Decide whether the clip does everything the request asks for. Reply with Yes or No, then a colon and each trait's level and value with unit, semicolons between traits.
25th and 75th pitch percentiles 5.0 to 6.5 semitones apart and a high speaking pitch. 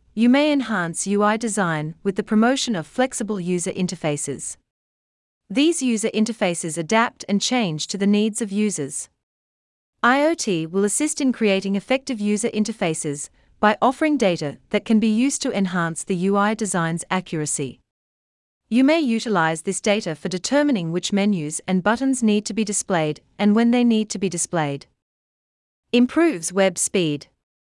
Yes: wide, 5.6 semitones; high, 200 Hz